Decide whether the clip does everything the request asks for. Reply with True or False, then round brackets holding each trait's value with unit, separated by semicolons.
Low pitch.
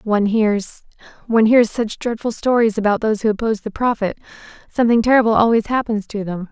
False (220 Hz)